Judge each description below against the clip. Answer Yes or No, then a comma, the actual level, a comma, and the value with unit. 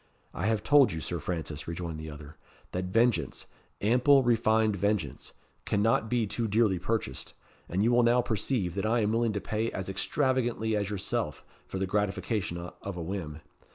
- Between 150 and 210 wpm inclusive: Yes, average, 175 wpm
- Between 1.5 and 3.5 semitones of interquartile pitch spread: No, average, 4.4 semitones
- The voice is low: Yes, low, 105 Hz